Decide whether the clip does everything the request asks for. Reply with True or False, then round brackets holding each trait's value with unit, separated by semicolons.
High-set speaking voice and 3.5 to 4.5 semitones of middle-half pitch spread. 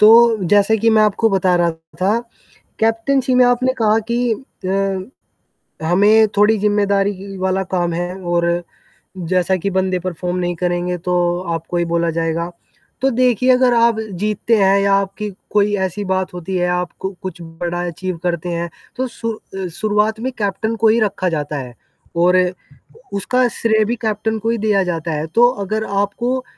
True (195 Hz; 3.8 semitones)